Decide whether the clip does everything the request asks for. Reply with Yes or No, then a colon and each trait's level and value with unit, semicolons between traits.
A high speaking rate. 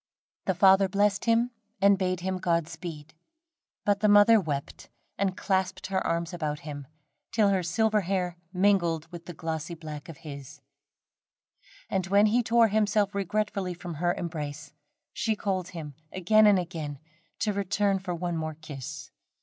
No: average, 155 wpm